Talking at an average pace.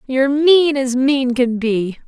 Yes: average, 175 wpm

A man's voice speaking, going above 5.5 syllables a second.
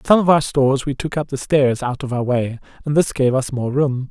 No: male; 5.4 syllables/s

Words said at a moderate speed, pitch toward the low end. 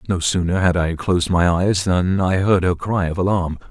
No: fast, 225 wpm; very low, 90 Hz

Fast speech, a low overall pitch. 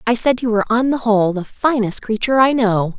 No: fast, 240 wpm; high, 230 Hz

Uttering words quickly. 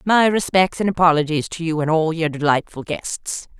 No: average, 185 wpm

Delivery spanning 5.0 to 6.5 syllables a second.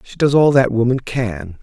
No: 4.6 syllables/s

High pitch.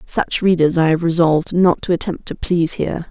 No: medium, 170 Hz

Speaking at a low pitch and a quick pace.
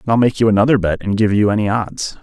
Yes: low, 105 Hz; fast, 295 wpm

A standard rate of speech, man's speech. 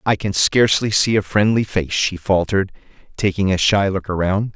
Yes: average, 185 wpm; male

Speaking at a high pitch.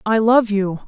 Yes: high, 215 Hz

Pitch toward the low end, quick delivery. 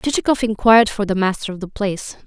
No: high, 210 Hz; fast, 210 wpm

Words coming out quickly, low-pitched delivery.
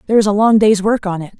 No: fast, 345 wpm; high, 205 Hz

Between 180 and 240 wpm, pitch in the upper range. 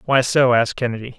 No: average, 200 wpm; low, 125 Hz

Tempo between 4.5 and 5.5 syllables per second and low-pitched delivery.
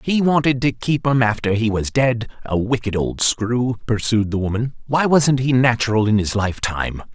Yes: 5.1 syllables/s; low, 115 Hz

